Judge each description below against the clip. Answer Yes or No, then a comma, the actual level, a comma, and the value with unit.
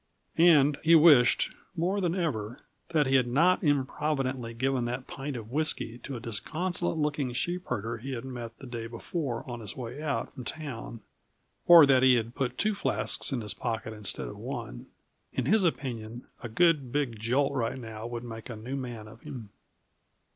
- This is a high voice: No, low, 130 Hz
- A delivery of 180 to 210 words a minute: Yes, average, 185 wpm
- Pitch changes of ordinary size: Yes, average, 4.4 semitones